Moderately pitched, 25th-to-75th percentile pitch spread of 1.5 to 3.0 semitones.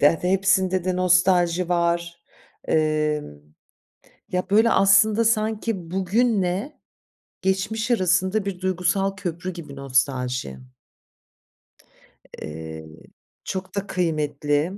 No: medium, 180 Hz; average, 3.8 semitones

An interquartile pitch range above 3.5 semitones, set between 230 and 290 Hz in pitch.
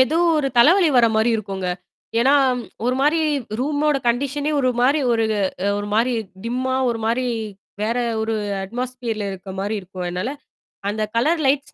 Yes: average, 4.1 semitones; high, 245 Hz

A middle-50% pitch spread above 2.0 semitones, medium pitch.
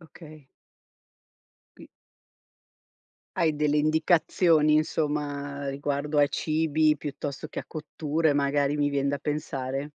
No: narrow, 1.5 semitones; medium, 150 Hz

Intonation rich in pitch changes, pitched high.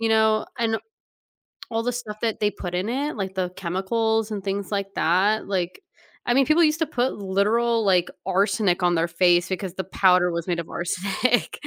No: average, 3.8 semitones; high, 200 Hz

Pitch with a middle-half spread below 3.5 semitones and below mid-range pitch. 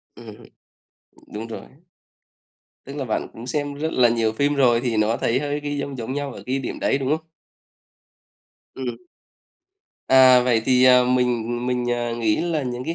Yes: average, 2.9 semitones; low, 125 Hz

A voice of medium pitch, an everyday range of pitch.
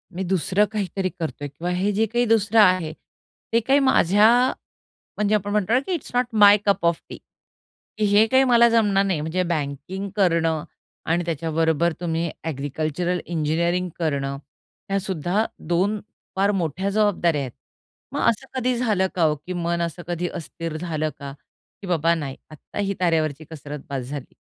Yes: medium, 175 Hz; average, 4.3 semitones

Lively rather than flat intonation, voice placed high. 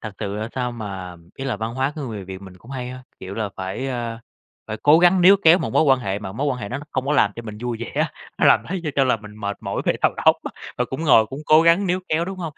No: wide, 5.8 semitones; low, 125 Hz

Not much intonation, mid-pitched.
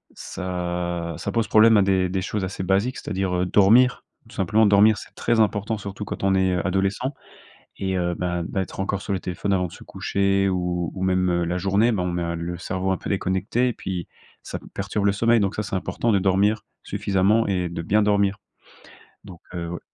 No: narrow, 2.2 semitones; very low, 95 Hz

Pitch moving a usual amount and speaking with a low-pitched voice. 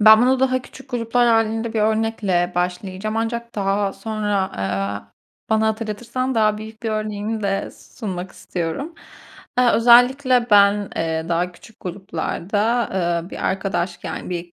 No: average, 3.5 semitones; high, 215 Hz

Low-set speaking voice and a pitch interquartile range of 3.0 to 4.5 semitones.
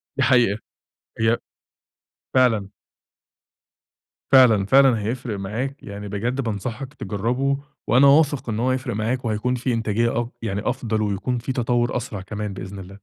Yes: low, 115 Hz; average, 3.6 semitones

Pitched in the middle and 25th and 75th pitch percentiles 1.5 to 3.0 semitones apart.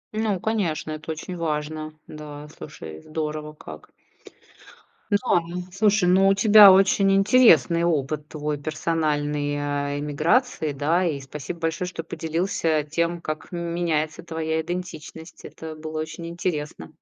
Yes: medium, 160 Hz; narrow, 2.6 semitones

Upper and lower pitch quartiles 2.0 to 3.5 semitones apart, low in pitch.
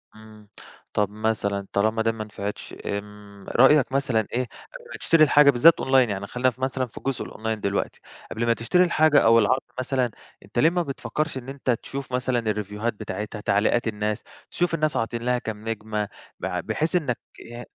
No: average, 4.1 semitones; low, 115 Hz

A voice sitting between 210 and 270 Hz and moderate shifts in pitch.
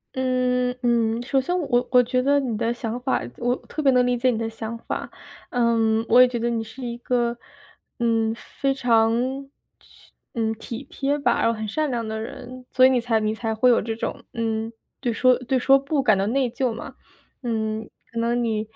No: high, 240 Hz; narrow, 2.1 semitones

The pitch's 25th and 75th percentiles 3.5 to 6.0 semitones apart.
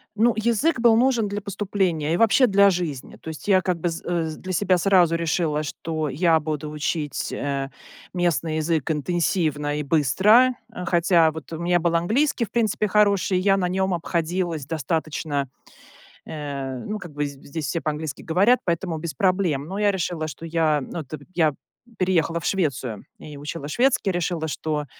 Yes: average, 3.9 semitones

